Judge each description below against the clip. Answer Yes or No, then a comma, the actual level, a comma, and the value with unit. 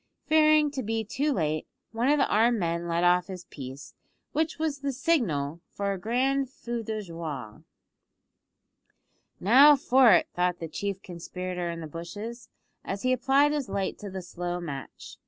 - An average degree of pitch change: No, wide, 7.5 semitones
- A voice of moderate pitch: No, high, 200 Hz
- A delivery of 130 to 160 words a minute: No, average, 170 wpm